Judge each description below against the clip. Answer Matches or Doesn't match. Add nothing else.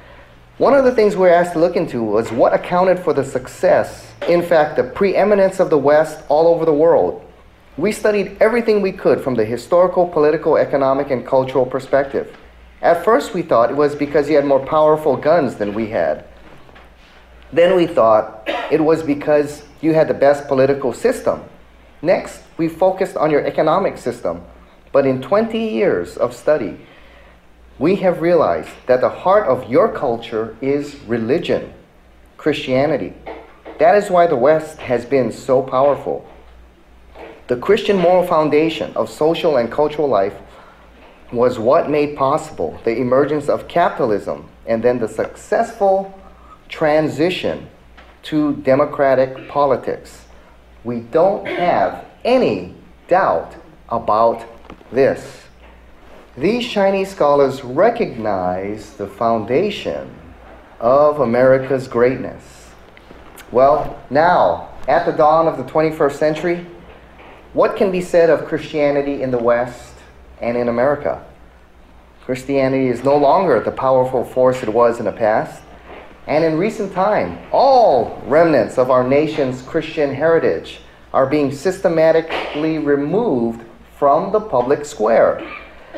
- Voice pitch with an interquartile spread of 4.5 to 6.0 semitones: Matches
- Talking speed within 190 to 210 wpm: Doesn't match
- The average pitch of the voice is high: Doesn't match